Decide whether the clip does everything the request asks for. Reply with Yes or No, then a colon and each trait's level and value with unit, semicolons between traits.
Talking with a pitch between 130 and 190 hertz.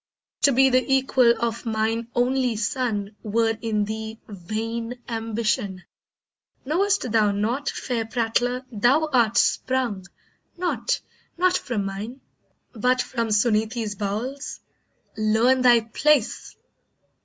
No: high, 230 Hz